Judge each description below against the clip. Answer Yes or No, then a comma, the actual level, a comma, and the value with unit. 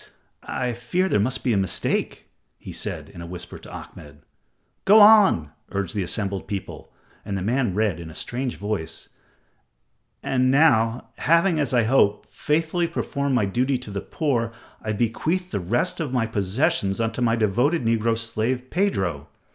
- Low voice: Yes, low, 115 Hz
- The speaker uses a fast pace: No, average, 165 wpm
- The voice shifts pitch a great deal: Yes, wide, 5.7 semitones